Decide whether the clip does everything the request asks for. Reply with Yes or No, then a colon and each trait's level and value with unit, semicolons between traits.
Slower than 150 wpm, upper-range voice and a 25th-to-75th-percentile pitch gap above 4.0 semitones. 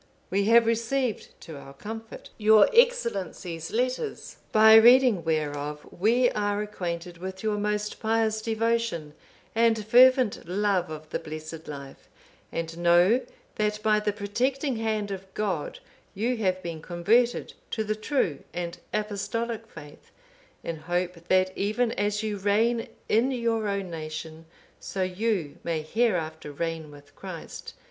Yes: average, 140 wpm; high, 205 Hz; average, 5.0 semitones